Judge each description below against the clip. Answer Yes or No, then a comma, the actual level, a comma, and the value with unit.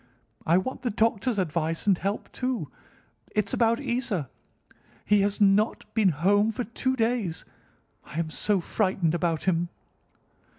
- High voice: Yes, high, 200 Hz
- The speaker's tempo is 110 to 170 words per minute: Yes, average, 140 wpm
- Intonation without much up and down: No, average, 4.8 semitones